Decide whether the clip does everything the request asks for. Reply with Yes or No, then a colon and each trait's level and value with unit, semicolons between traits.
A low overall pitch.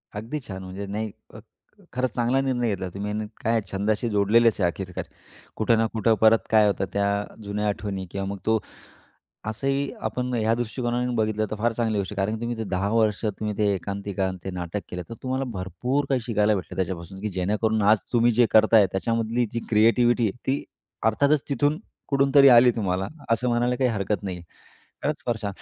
Yes: low, 110 Hz